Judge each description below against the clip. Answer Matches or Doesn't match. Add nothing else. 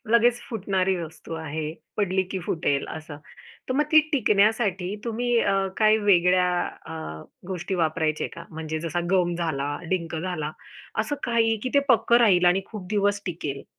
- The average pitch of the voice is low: Doesn't match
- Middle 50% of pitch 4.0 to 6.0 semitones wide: Matches